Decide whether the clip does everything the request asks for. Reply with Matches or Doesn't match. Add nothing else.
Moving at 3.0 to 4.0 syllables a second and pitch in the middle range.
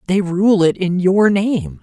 Matches